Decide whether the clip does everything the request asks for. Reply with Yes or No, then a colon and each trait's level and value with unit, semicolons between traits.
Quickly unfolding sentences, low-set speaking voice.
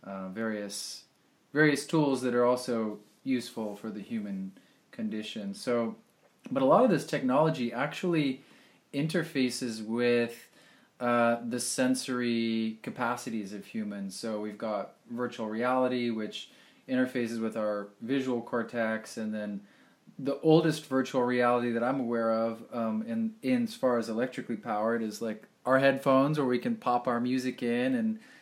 No: average, 150 wpm; low, 120 Hz